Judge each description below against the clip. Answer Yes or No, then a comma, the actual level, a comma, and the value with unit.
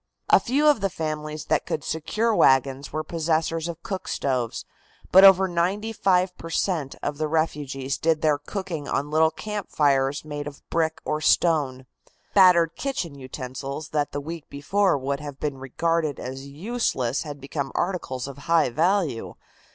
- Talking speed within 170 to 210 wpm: No, average, 160 wpm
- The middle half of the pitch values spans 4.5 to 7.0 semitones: No, average, 3.8 semitones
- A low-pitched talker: No, medium, 155 Hz